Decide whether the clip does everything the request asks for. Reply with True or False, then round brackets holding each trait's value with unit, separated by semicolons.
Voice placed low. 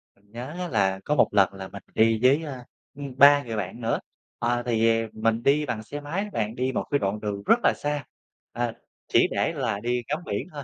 True (120 Hz)